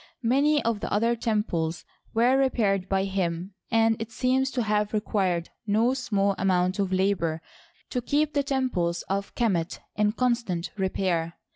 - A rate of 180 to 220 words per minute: No, average, 150 wpm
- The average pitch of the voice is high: Yes, high, 210 Hz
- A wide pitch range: No, average, 4.3 semitones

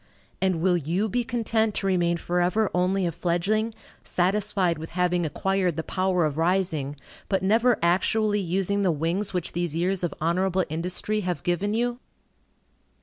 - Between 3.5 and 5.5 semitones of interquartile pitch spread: No, average, 2.9 semitones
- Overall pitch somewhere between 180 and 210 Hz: Yes, medium, 185 Hz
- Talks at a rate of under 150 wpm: No, average, 155 wpm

